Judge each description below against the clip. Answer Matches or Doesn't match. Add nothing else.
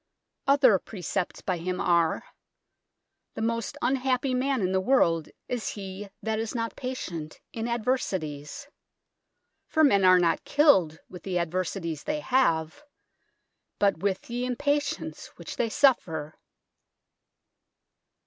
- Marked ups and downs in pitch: Matches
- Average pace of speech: Doesn't match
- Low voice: Doesn't match